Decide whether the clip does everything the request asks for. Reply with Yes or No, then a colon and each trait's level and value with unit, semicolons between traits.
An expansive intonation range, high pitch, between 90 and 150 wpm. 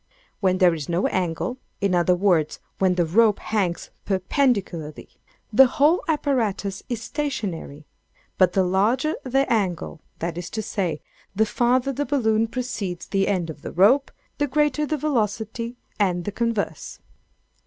Yes: wide, 5.8 semitones; high, 205 Hz; average, 145 wpm